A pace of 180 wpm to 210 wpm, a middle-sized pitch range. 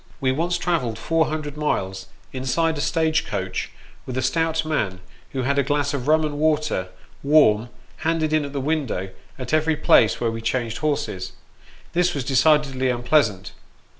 No: average, 165 wpm; average, 4.3 semitones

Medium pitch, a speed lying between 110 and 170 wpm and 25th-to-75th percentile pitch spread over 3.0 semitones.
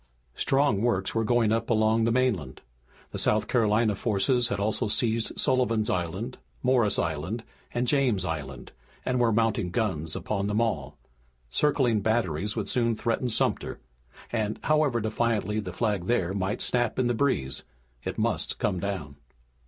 No: low, 110 Hz; average, 150 wpm; average, 3.6 semitones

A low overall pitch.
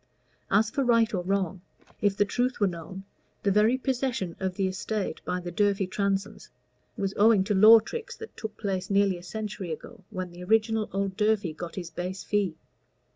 No: high, 200 Hz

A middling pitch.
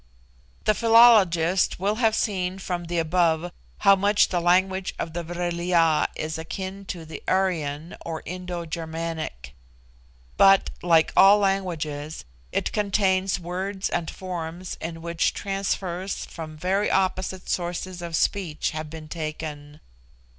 Yes: medium, 175 Hz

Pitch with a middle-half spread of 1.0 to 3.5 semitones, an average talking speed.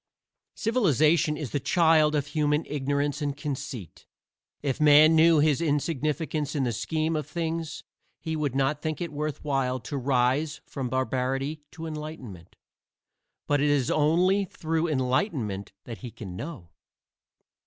Yes: average, 3.0 semitones; average, 145 wpm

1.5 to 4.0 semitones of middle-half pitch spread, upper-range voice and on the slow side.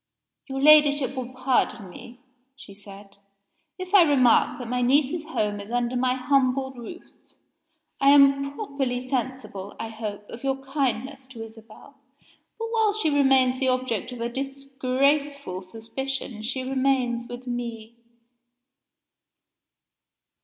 Yes: average, 2.7 semitones; very high, 255 Hz; slow, 130 wpm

